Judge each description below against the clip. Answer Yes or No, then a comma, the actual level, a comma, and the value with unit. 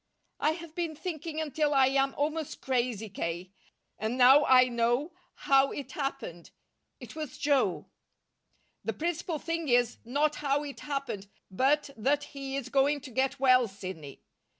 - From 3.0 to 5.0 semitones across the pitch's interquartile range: Yes, average, 3.5 semitones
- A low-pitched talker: No, very high, 275 Hz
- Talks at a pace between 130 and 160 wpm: Yes, average, 150 wpm